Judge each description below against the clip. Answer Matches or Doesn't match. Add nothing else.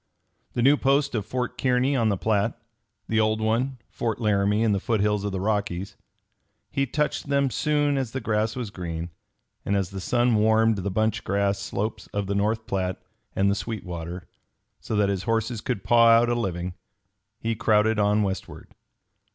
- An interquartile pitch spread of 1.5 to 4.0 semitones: Matches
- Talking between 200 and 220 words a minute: Doesn't match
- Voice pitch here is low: Matches